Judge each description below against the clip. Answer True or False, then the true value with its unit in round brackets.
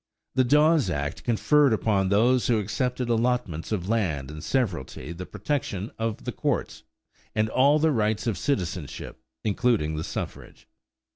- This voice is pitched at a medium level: False (110 Hz)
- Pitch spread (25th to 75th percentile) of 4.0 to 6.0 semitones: True (5.6 semitones)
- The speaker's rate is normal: True (145 wpm)